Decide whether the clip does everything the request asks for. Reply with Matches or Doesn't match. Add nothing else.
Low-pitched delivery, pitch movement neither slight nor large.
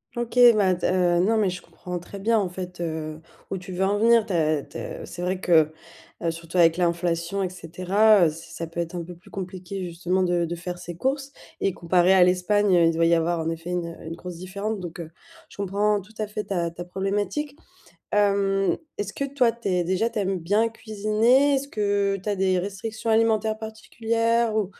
Doesn't match